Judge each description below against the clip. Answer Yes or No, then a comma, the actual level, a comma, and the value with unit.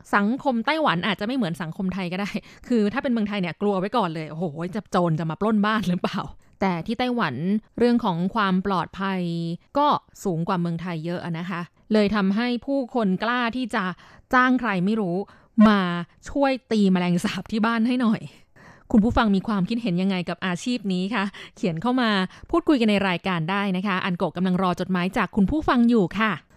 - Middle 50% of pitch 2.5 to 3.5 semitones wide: No, average, 4.0 semitones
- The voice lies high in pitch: Yes, high, 200 Hz